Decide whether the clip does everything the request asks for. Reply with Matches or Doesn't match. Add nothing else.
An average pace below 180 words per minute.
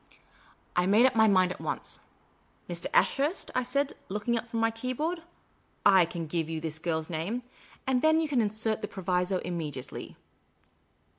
Matches